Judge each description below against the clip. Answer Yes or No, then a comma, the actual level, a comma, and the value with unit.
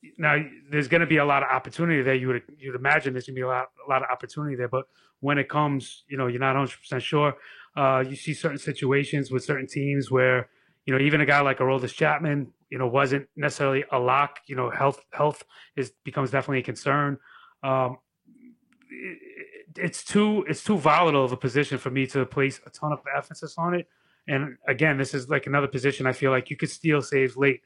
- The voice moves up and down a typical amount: No, narrow, 2.2 semitones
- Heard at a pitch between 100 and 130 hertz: No, medium, 140 Hz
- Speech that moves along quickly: Yes, fast, 225 wpm